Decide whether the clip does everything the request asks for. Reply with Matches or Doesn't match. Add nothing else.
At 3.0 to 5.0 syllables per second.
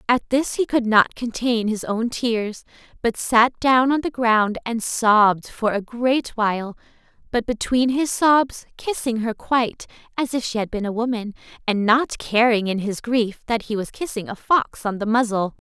Matches